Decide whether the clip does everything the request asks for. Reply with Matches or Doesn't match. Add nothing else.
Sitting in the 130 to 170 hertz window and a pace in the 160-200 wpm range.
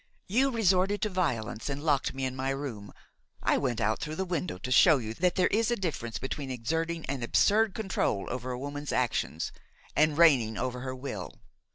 Matches